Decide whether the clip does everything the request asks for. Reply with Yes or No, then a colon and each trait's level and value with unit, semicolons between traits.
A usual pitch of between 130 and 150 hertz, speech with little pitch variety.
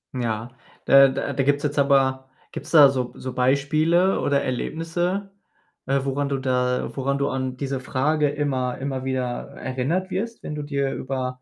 Yes: low, 135 Hz; narrow, 2.1 semitones